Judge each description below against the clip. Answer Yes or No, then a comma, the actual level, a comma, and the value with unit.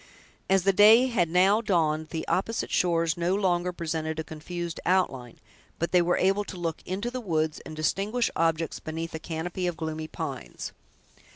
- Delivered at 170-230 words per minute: Yes, average, 175 wpm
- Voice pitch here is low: No, medium, 175 Hz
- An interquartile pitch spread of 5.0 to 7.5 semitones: No, average, 3.1 semitones